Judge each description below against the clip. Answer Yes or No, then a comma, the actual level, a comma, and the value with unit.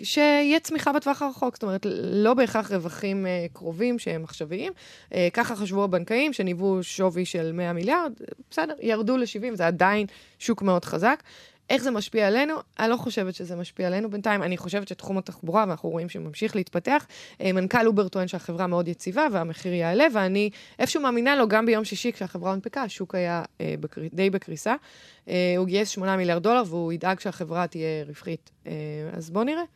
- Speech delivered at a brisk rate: Yes, fast, 160 wpm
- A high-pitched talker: Yes, high, 195 Hz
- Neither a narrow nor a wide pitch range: Yes, average, 4.9 semitones